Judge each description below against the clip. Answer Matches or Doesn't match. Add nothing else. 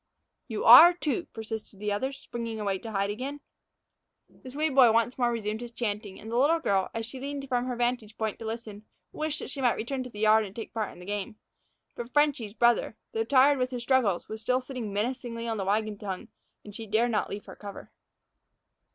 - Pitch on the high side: Matches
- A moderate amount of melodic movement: Matches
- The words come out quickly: Matches